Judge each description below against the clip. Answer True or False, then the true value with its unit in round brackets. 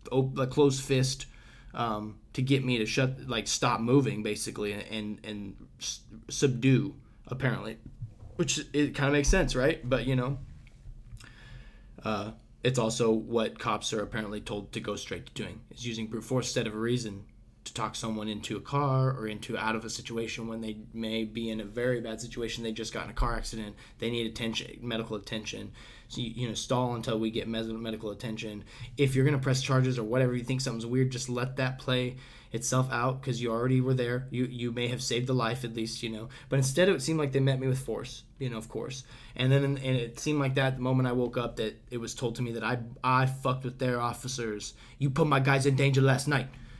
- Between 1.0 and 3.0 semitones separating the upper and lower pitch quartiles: True (2.7 semitones)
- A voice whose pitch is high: False (120 Hz)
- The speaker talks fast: True (220 wpm)